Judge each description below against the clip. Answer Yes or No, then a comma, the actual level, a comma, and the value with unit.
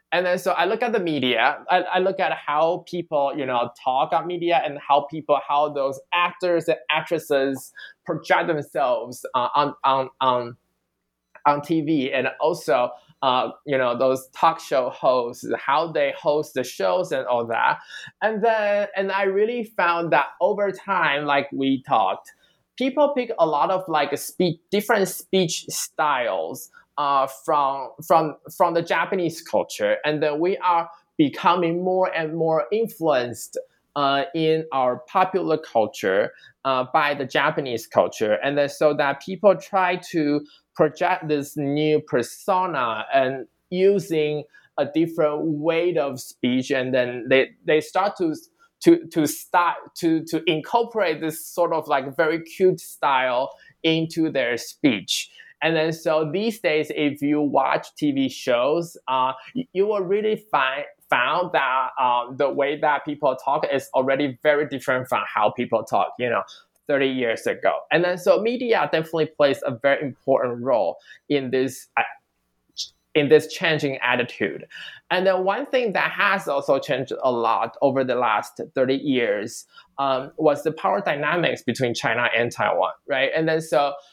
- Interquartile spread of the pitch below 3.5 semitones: No, average, 4.8 semitones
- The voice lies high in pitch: No, medium, 155 Hz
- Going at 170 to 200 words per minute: No, average, 160 wpm